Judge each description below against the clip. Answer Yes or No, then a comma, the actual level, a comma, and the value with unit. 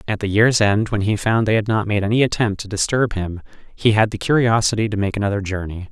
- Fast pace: Yes, fast, 245 wpm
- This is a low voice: Yes, low, 105 Hz